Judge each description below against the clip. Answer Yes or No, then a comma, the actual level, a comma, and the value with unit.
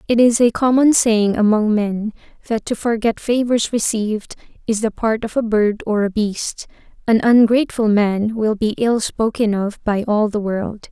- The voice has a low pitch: No, high, 220 Hz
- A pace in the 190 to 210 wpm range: No, average, 180 wpm